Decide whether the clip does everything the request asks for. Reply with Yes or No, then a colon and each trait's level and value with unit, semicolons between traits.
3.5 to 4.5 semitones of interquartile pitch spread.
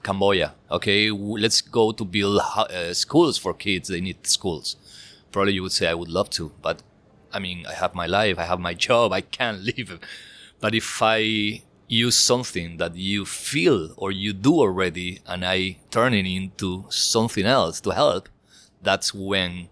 No: narrow, 2.6 semitones